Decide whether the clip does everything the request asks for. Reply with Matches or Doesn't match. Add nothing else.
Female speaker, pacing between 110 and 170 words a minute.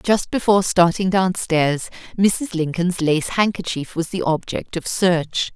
Matches